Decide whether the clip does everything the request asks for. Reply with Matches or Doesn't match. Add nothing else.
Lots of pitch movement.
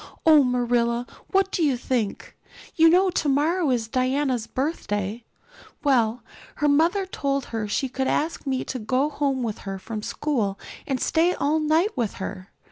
Doesn't match